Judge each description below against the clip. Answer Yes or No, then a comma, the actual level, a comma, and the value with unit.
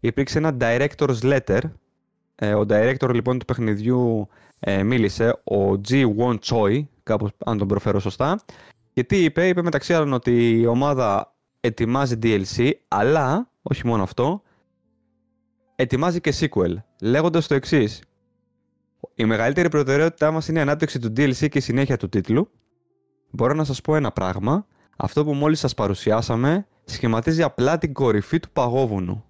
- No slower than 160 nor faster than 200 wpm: No, average, 150 wpm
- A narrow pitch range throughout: No, wide, 5.4 semitones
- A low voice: Yes, low, 130 Hz